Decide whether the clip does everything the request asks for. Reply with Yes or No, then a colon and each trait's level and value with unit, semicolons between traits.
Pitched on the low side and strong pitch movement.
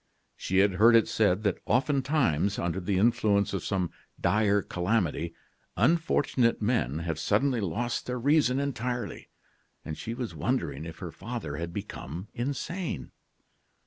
Yes: low, 105 Hz; wide, 5.7 semitones